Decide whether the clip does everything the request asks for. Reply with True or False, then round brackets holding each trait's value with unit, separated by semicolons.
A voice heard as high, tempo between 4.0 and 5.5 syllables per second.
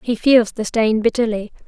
True (225 Hz; 4.8 syllables/s)